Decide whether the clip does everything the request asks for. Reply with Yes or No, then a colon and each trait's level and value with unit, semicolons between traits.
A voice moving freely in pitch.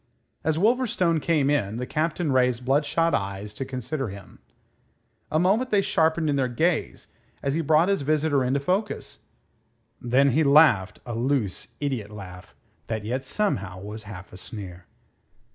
Yes: wide, 6.6 semitones